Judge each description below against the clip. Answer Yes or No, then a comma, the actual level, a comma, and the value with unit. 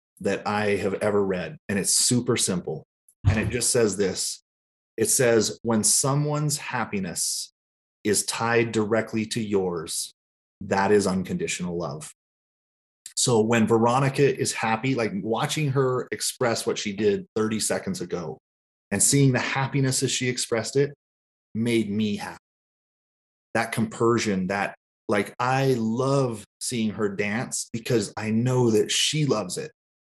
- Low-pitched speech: Yes, low, 115 Hz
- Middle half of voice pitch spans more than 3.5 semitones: Yes, average, 3.9 semitones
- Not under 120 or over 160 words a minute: Yes, average, 140 wpm